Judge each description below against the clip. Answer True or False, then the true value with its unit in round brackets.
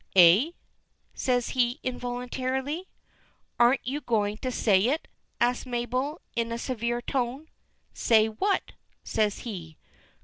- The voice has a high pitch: True (245 Hz)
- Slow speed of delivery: True (115 wpm)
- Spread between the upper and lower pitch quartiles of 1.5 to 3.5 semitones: True (2.7 semitones)